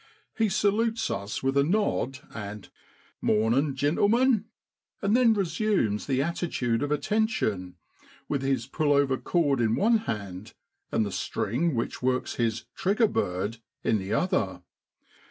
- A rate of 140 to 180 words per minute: Yes, average, 150 wpm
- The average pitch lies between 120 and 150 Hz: Yes, medium, 140 Hz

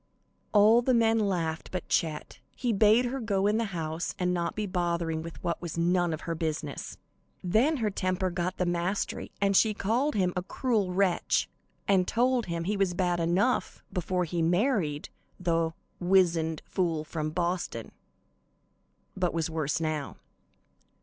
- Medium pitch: Yes, medium, 180 Hz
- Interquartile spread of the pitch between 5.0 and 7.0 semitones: No, average, 3.6 semitones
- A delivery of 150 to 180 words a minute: Yes, average, 160 wpm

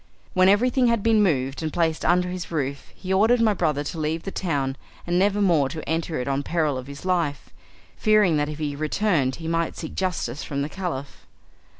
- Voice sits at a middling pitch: Yes, medium, 165 Hz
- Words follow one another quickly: Yes, fast, 210 wpm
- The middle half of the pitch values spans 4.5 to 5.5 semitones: Yes, average, 4.8 semitones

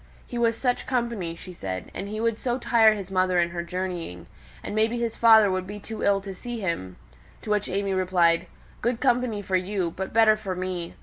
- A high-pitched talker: Yes, high, 200 Hz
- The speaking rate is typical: No, fast, 210 wpm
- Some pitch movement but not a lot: Yes, average, 3.8 semitones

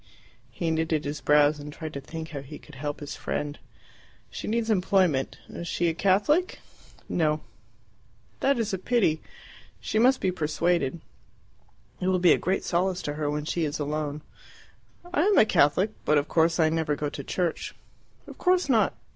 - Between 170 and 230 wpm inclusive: Yes, average, 180 wpm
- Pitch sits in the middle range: Yes, medium, 160 Hz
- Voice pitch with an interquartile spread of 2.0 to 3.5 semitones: No, average, 4.2 semitones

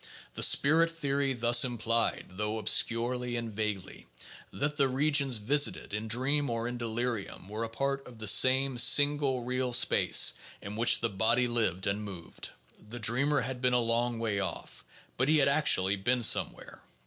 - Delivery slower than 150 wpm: No, average, 175 wpm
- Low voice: Yes, low, 120 Hz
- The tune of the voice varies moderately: Yes, average, 3.5 semitones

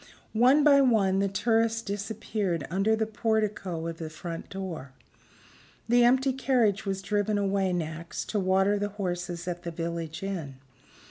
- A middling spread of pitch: Yes, average, 4.0 semitones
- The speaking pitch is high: Yes, high, 195 Hz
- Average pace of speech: Yes, average, 150 wpm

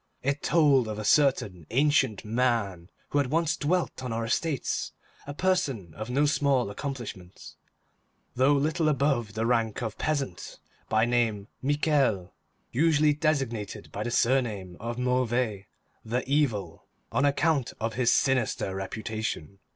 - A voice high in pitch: No, low, 125 Hz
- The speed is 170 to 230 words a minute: No, slow, 135 wpm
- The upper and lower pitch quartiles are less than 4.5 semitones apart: No, average, 4.8 semitones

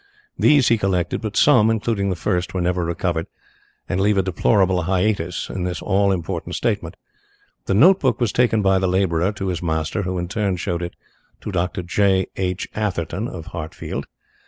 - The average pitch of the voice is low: Yes, very low, 95 Hz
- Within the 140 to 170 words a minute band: No, average, 180 wpm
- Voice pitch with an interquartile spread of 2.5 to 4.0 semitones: Yes, average, 2.8 semitones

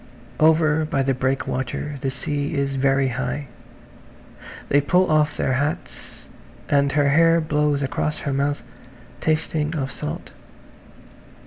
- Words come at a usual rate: No, slow, 125 wpm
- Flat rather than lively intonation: Yes, narrow, 2.1 semitones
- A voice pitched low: No, medium, 145 Hz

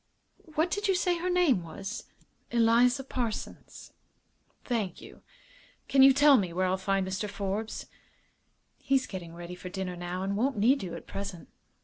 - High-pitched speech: Yes, high, 210 Hz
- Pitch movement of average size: No, wide, 6.2 semitones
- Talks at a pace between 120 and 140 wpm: No, average, 160 wpm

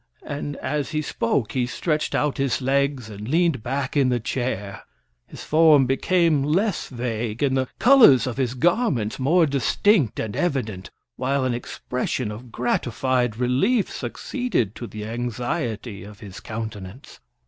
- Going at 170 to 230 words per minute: No, average, 150 wpm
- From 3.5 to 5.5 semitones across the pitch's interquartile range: Yes, average, 4.3 semitones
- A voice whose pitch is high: No, low, 130 Hz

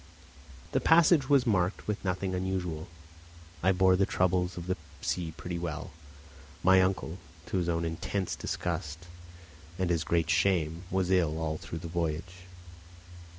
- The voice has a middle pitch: No, very low, 90 Hz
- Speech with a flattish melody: Yes, narrow, 2.2 semitones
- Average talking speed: Yes, average, 150 wpm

